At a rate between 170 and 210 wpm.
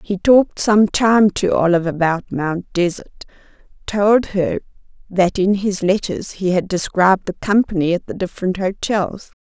No: average, 155 wpm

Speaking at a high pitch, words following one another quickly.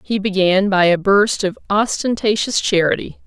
No: high, 200 Hz; average, 145 wpm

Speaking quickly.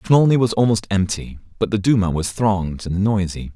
No: average, 185 wpm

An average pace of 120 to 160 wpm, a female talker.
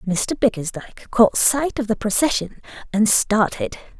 Yes: slow, 135 wpm; female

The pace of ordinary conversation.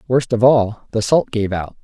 No: fast, 230 wpm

